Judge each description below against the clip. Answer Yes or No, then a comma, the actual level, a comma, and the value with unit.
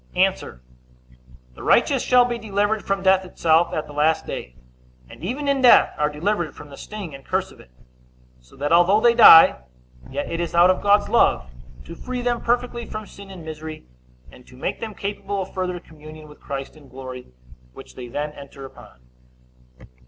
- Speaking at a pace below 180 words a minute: No, average, 190 wpm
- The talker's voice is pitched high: No, medium, 175 Hz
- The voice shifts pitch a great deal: Yes, wide, 5.9 semitones